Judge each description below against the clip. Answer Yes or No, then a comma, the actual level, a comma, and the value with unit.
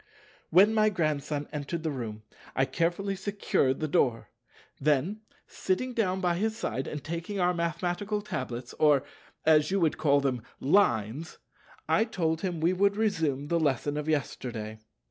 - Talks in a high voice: No, medium, 160 Hz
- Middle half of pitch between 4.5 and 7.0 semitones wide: Yes, average, 5.2 semitones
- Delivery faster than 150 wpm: No, average, 145 wpm